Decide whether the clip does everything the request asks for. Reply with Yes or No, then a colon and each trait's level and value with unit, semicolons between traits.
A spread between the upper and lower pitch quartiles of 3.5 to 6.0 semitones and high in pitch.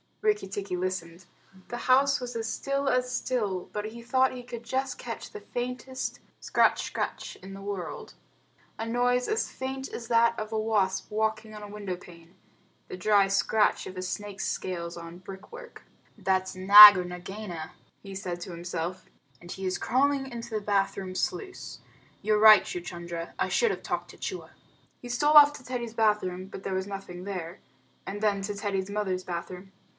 Yes: average, 4.6 semitones; high, 205 Hz